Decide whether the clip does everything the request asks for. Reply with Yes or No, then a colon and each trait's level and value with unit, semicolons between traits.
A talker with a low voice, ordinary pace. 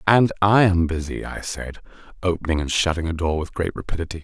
Yes: very low, 85 Hz; average, 185 wpm